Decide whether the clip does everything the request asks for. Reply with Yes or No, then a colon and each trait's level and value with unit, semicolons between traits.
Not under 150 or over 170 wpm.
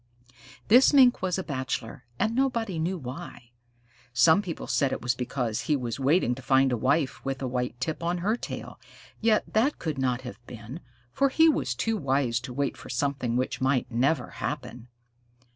No: average, 185 wpm